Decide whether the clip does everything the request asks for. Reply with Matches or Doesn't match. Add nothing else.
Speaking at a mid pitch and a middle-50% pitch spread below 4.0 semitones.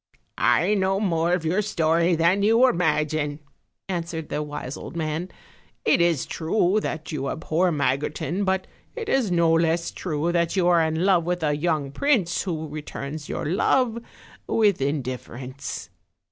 Matches